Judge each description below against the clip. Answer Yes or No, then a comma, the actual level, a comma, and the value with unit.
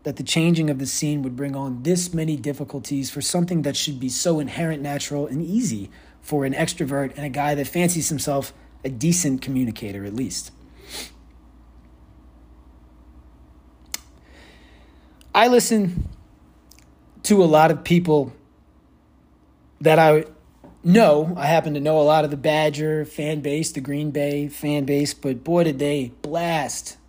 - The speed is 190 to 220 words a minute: No, average, 150 wpm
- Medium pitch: Yes, medium, 145 Hz